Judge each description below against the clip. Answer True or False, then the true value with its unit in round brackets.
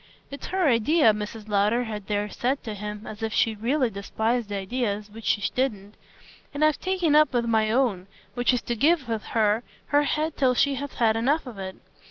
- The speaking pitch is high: True (230 Hz)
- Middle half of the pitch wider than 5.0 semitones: False (4.4 semitones)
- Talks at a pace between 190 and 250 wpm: True (200 wpm)